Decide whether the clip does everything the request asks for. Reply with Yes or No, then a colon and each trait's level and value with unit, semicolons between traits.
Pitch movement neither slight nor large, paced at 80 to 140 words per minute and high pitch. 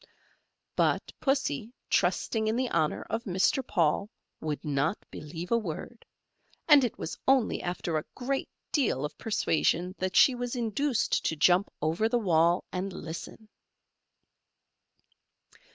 No: wide, 6.7 semitones; slow, 135 wpm; high, 195 Hz